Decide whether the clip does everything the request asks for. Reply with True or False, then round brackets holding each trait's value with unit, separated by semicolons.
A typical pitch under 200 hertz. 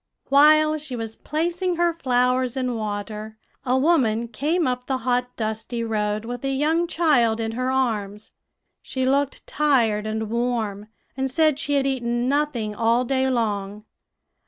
False (250 Hz)